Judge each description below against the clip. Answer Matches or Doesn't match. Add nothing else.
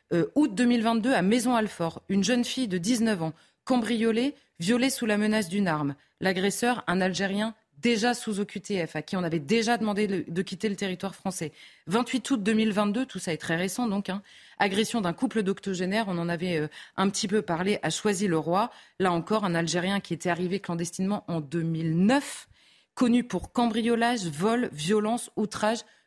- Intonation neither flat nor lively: Matches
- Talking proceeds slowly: Doesn't match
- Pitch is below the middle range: Doesn't match